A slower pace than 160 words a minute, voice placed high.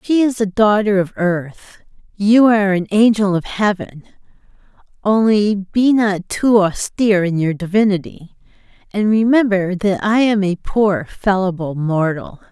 Yes: average, 140 wpm; high, 200 Hz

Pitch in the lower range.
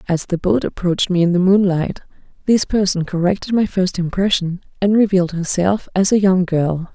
No: medium, 185 Hz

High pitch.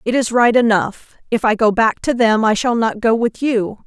Yes: high, 230 Hz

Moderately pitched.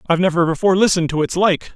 Yes: medium, 175 Hz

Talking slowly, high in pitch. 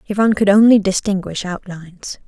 Yes: slow, 130 wpm; high, 195 Hz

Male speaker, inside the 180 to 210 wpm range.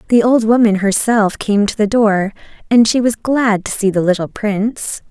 No: female; average, 200 wpm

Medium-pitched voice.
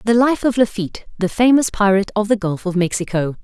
No: high, 205 Hz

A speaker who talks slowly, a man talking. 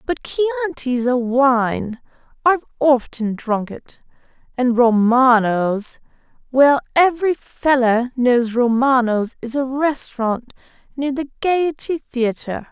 No: slow, 100 wpm; female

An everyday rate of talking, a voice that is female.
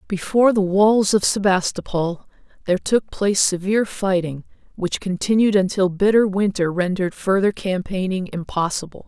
No: slow, 125 wpm; female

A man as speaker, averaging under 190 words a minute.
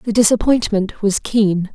No: female; average, 140 wpm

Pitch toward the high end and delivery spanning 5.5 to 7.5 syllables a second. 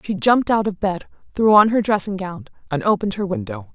Yes: high, 205 Hz; 6.1 syllables/s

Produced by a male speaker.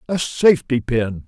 Yes: male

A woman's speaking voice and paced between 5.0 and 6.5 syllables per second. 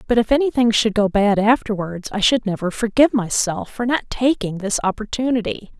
Yes: female; 5.5 syllables/s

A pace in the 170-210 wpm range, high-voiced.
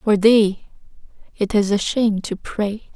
No: average, 160 wpm; high, 210 Hz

